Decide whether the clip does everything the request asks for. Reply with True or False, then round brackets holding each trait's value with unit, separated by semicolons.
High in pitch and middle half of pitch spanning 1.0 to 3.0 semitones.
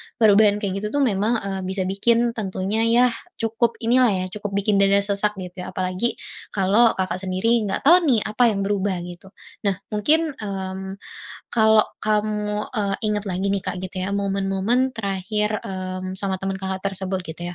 True (200 Hz; 2.4 semitones)